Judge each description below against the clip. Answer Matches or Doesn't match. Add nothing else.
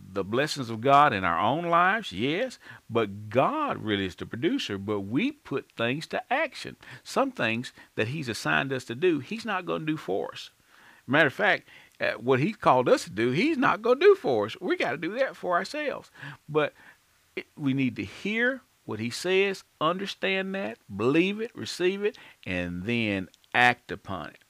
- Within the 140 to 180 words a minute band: Doesn't match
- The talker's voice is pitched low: Doesn't match